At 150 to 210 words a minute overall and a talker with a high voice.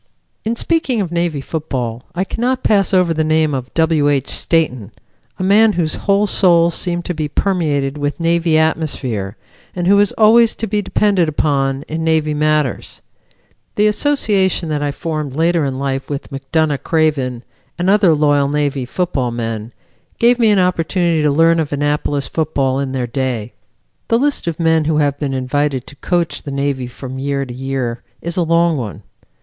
No: average, 175 wpm; medium, 155 Hz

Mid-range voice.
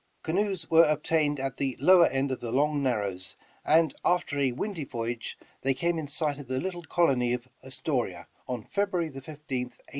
Yes: medium, 145 Hz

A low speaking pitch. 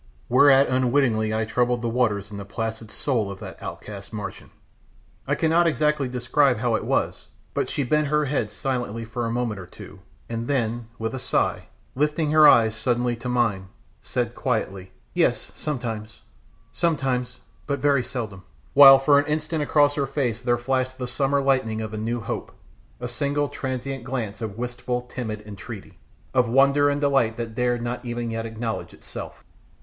Yes: low, 125 Hz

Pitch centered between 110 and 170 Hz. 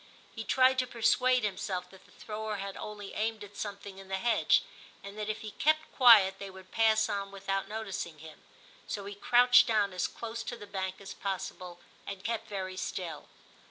No: high, 205 Hz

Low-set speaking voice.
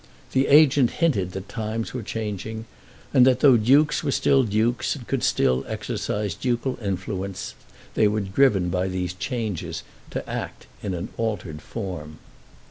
Yes: low, 110 Hz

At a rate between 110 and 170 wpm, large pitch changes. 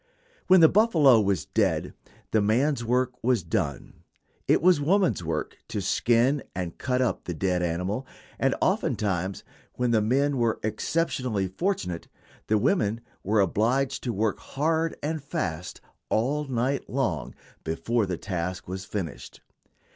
Yes: average, 140 wpm; wide, 6.7 semitones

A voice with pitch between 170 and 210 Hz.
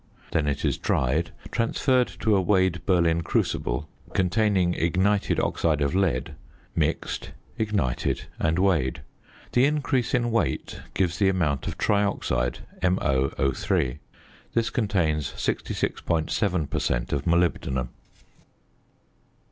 No: very low, 90 Hz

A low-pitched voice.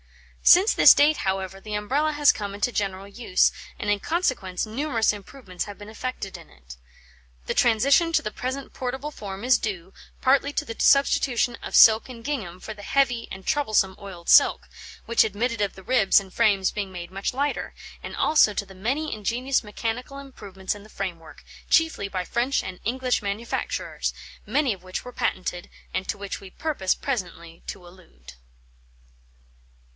No: high, 215 Hz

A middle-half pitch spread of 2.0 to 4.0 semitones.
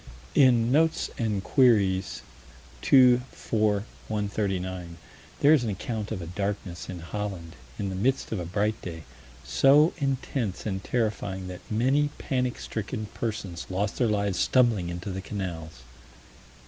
No: average, 4.5 semitones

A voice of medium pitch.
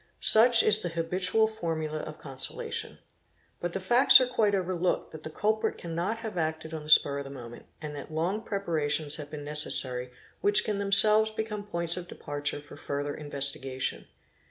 Yes: medium, 165 Hz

